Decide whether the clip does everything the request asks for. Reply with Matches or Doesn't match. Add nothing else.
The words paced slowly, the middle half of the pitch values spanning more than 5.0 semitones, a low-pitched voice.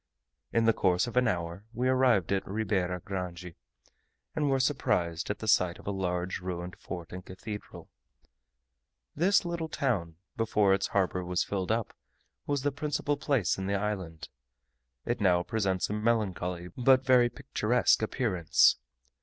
Doesn't match